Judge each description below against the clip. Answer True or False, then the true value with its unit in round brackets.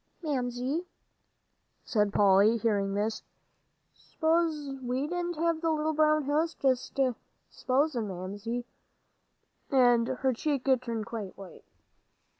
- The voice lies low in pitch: False (255 Hz)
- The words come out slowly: True (105 wpm)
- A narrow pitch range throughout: False (5.5 semitones)